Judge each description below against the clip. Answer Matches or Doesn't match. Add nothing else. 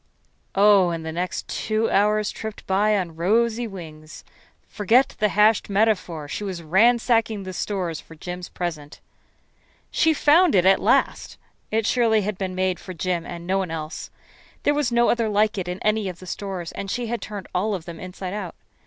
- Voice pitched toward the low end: Doesn't match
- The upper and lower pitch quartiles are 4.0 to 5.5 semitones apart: Doesn't match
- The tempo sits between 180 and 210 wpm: Matches